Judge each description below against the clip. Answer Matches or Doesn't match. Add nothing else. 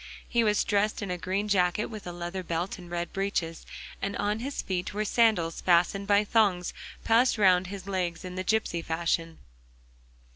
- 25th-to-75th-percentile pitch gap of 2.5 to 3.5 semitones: Matches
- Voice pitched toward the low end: Doesn't match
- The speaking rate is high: Doesn't match